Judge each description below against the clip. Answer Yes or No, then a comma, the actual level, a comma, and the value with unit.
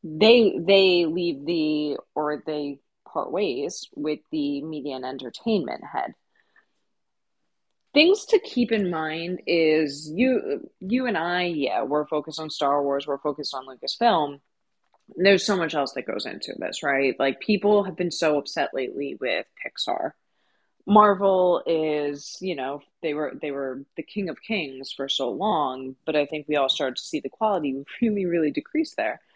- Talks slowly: No, average, 165 wpm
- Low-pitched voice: No, medium, 155 Hz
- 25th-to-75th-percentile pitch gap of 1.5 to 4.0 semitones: No, wide, 5.5 semitones